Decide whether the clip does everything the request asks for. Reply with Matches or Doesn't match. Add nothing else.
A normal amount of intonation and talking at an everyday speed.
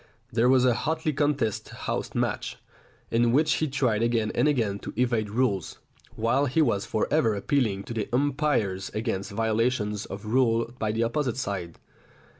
Matches